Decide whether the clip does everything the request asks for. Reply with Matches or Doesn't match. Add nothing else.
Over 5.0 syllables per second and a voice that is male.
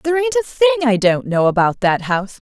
Doesn't match